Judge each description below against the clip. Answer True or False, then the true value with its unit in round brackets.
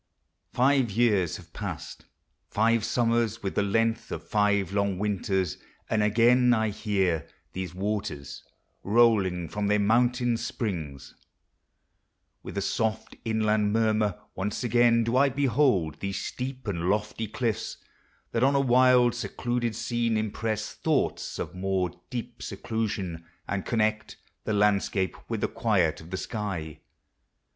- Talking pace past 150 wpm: False (135 wpm)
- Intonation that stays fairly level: False (3.3 semitones)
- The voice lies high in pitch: False (110 Hz)